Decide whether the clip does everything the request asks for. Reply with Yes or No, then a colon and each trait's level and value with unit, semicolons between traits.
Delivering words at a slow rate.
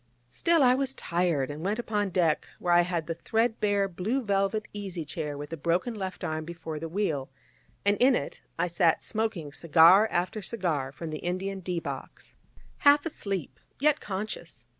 No: average, 170 wpm